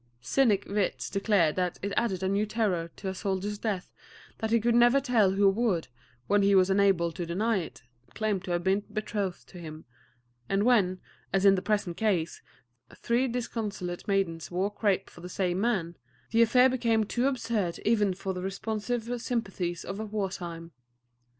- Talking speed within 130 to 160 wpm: No, average, 175 wpm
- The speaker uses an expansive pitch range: No, average, 3.3 semitones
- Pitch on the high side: Yes, high, 200 Hz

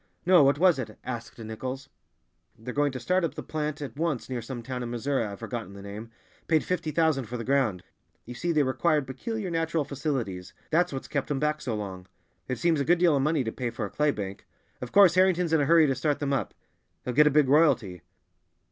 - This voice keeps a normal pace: No, fast, 230 wpm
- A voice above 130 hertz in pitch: Yes, medium, 140 Hz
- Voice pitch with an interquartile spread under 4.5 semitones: No, average, 4.8 semitones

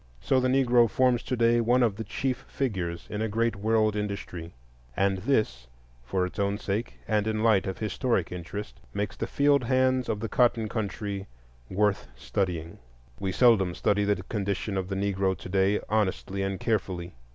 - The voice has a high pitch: No, low, 105 Hz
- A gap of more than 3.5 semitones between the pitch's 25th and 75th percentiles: No, average, 3.2 semitones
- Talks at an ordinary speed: Yes, average, 180 wpm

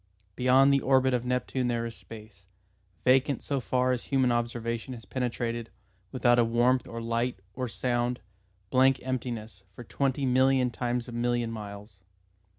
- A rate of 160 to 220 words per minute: No, average, 150 wpm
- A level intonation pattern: Yes, narrow, 1.7 semitones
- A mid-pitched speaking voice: No, low, 120 Hz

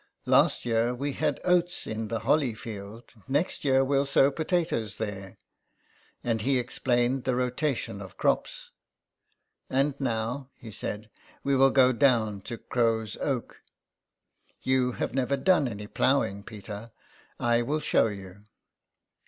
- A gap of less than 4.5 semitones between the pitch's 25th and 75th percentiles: Yes, average, 3.7 semitones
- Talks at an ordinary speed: Yes, average, 145 wpm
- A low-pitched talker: Yes, low, 120 Hz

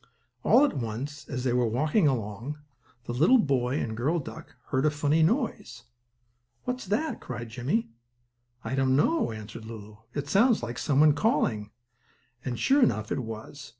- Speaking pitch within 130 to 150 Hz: Yes, low, 135 Hz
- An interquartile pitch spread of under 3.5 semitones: No, average, 5.1 semitones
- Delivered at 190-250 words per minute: No, average, 165 wpm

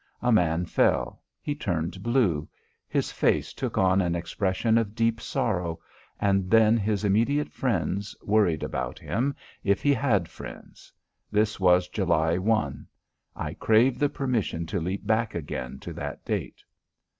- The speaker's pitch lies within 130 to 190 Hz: No, low, 100 Hz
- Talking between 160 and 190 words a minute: No, average, 145 wpm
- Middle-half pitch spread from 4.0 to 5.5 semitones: Yes, average, 4.5 semitones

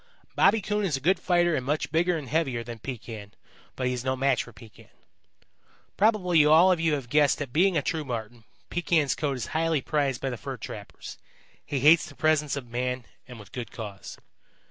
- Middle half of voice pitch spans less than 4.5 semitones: No, average, 4.9 semitones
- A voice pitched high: No, medium, 140 Hz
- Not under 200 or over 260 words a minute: Yes, fast, 205 wpm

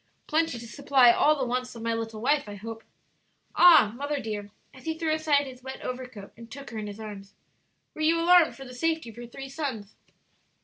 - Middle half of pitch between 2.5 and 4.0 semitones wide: No, average, 4.8 semitones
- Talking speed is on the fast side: Yes, fast, 215 wpm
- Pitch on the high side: Yes, very high, 255 Hz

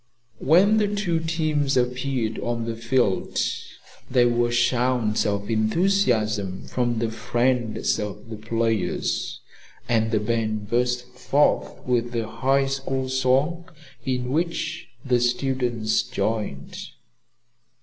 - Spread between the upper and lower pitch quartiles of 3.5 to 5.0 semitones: No, average, 3.0 semitones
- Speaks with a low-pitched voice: Yes, low, 120 Hz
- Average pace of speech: No, slow, 115 wpm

